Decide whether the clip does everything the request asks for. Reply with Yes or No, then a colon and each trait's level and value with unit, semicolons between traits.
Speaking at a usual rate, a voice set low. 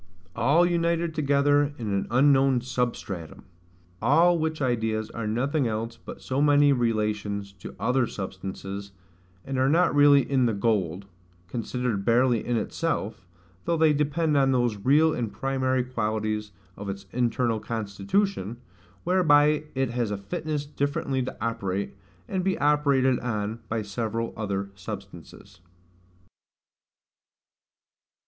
No: slow, 125 wpm; low, 125 Hz